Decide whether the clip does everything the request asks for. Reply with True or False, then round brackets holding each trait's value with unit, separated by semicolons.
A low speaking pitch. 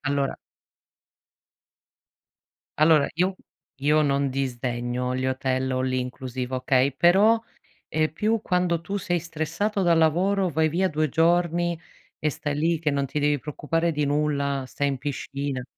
False (150 Hz)